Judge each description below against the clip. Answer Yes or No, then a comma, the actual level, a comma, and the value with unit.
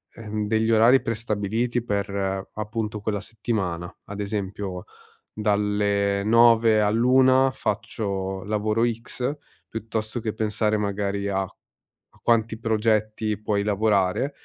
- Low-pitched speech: Yes, low, 105 Hz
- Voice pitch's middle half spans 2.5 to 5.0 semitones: No, narrow, 2.0 semitones